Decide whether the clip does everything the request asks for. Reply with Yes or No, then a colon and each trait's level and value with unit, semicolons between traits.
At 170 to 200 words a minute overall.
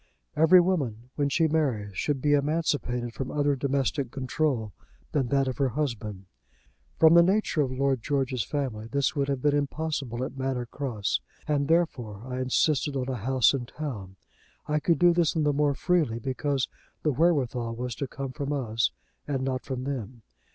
Yes: average, 175 wpm